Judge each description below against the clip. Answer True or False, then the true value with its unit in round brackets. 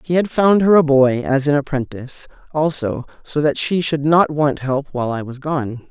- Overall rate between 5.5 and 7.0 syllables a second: False (5.0 syllables/s)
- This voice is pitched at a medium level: True (145 Hz)